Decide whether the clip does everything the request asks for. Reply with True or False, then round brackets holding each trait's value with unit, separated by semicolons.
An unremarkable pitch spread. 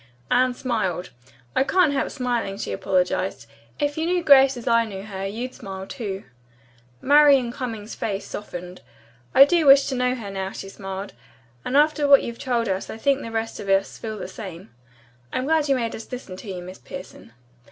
False (5.7 semitones)